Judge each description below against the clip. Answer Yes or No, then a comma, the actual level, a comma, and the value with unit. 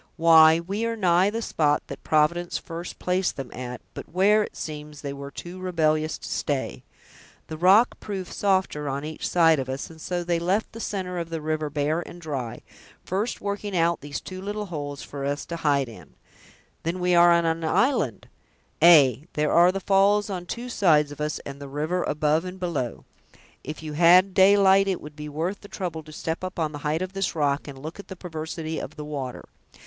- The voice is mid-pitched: Yes, medium, 165 Hz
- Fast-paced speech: Yes, fast, 210 wpm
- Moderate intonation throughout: Yes, average, 3.7 semitones